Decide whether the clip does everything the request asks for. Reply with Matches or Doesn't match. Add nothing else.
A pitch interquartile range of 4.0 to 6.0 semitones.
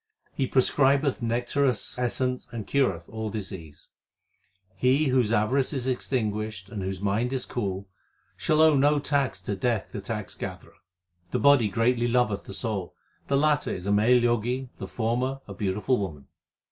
Matches